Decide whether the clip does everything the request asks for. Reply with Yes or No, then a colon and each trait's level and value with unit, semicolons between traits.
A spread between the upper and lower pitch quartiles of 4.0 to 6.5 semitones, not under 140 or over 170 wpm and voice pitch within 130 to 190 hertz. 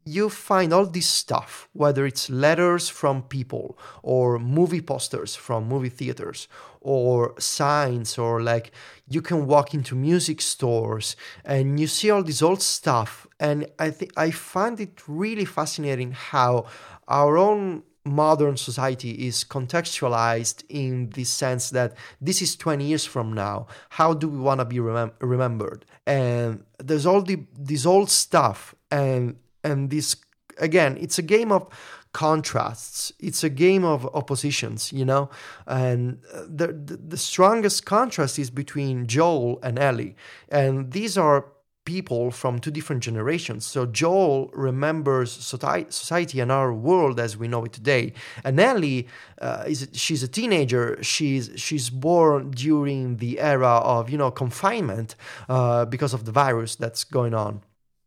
Yes: average, 4.4 semitones; average, 150 wpm; medium, 140 Hz